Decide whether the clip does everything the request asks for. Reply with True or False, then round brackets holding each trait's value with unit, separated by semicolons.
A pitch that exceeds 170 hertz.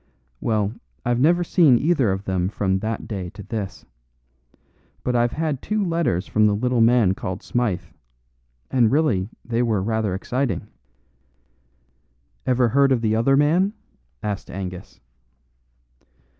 False (115 Hz)